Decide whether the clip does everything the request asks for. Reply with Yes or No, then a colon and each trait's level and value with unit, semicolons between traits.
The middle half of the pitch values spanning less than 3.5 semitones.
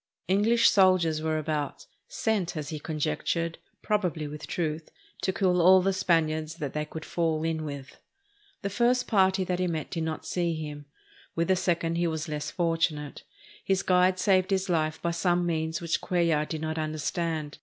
Yes: average, 2.9 semitones